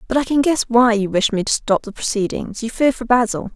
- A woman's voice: Yes, female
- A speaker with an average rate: No, fast, 255 wpm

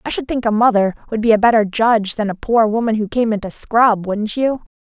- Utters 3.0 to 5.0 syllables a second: No, 5.6 syllables/s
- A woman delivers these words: Yes, female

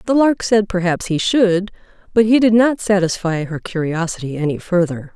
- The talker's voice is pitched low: No, high, 190 Hz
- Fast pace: No, average, 175 wpm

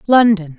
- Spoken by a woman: Yes, female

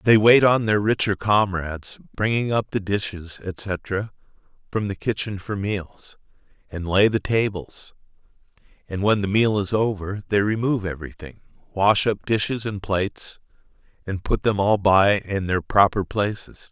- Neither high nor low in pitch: No, low, 100 Hz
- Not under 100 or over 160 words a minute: Yes, average, 155 wpm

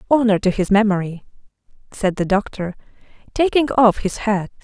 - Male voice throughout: No, female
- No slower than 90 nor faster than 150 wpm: Yes, average, 140 wpm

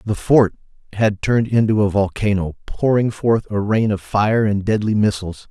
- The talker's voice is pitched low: Yes, low, 105 Hz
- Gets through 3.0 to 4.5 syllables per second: No, 4.9 syllables/s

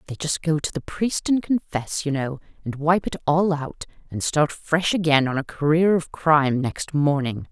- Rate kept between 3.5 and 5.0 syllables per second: Yes, 4.7 syllables/s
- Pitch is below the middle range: No, medium, 155 Hz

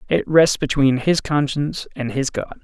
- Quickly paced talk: No, average, 185 wpm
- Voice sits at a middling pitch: Yes, medium, 145 Hz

